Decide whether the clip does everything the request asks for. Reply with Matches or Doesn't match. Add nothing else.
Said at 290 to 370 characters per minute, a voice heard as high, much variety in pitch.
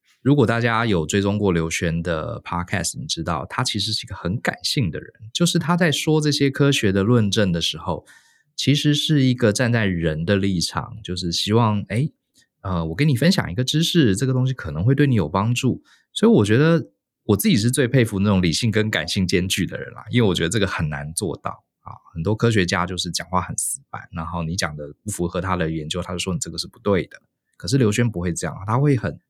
Doesn't match